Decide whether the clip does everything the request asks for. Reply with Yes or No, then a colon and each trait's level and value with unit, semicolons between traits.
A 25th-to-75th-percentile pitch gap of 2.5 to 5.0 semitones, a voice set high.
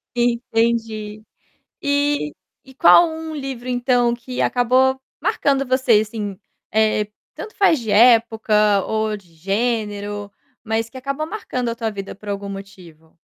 Yes: average, 3.7 semitones; high, 230 Hz